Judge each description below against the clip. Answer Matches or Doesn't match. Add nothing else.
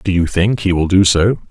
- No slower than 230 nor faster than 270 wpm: Doesn't match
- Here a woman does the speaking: Doesn't match